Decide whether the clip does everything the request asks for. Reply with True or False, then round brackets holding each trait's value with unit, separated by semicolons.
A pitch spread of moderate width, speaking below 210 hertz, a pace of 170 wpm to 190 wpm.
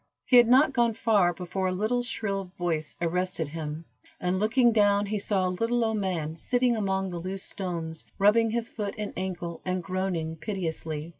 True (3.9 semitones; 190 Hz; 180 wpm)